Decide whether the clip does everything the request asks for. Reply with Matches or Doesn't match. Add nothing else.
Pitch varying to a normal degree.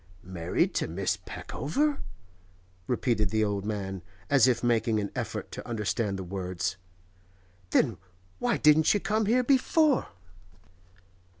Doesn't match